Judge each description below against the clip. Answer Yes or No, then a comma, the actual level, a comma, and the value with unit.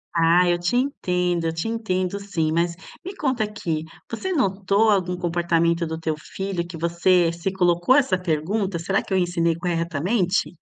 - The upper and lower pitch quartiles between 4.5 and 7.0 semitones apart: No, average, 2.9 semitones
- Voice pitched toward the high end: No, medium, 180 Hz